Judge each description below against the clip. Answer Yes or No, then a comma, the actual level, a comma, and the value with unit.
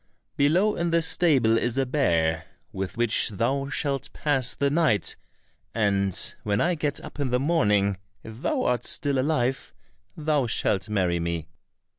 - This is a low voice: Yes, low, 125 Hz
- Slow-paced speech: No, average, 155 wpm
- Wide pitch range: Yes, wide, 6.3 semitones